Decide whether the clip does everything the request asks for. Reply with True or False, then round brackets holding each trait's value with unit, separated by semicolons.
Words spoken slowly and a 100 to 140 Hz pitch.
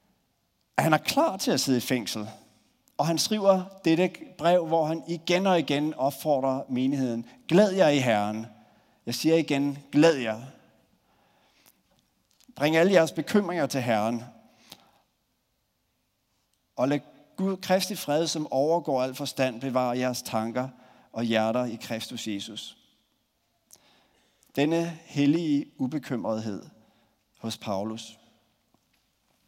True (115 wpm; 135 Hz)